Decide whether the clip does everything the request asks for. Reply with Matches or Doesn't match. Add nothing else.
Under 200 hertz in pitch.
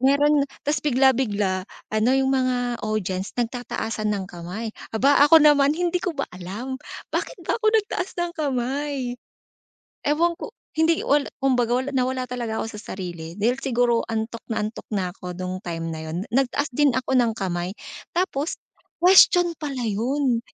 Doesn't match